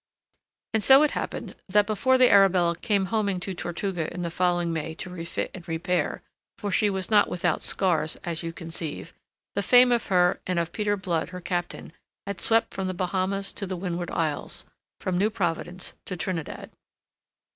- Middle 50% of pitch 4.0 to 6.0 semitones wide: No, average, 2.7 semitones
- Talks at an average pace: Yes, average, 180 wpm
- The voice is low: No, medium, 185 Hz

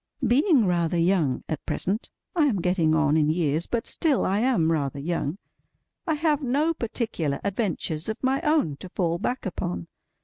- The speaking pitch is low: No, medium, 185 Hz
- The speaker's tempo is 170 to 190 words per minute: No, average, 160 wpm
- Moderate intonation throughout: No, wide, 8.3 semitones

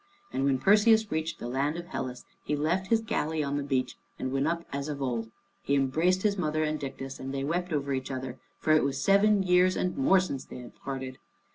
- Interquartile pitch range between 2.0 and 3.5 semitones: No, average, 5.1 semitones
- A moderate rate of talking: No, fast, 230 wpm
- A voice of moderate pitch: Yes, medium, 150 Hz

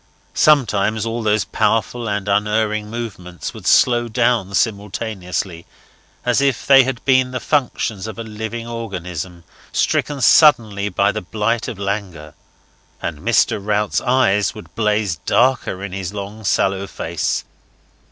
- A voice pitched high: No, low, 105 Hz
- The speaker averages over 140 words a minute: No, slow, 135 wpm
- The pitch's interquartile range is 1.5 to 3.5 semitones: Yes, average, 3.1 semitones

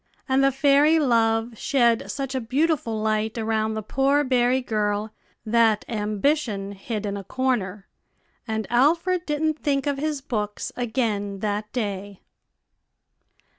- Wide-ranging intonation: No, average, 4.3 semitones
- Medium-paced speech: No, slow, 130 wpm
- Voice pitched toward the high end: Yes, high, 230 Hz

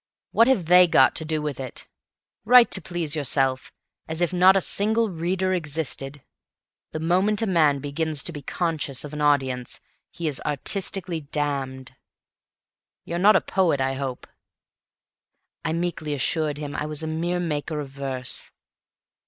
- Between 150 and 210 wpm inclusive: Yes, average, 160 wpm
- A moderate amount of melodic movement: Yes, average, 3.9 semitones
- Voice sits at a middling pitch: Yes, medium, 155 Hz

